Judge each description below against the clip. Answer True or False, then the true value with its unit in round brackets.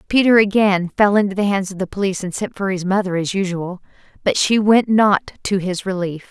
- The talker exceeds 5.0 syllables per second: True (5.5 syllables/s)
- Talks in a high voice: True (195 Hz)